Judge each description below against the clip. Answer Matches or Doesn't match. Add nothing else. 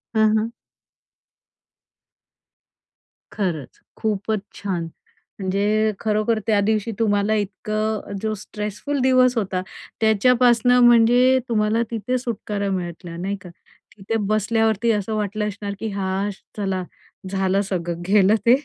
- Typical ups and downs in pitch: Doesn't match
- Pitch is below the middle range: Doesn't match